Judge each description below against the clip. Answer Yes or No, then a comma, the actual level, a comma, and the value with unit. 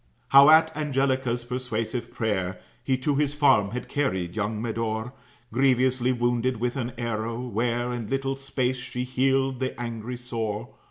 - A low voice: Yes, low, 125 Hz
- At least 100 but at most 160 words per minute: Yes, average, 150 wpm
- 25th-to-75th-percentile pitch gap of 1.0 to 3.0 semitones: Yes, narrow, 2.5 semitones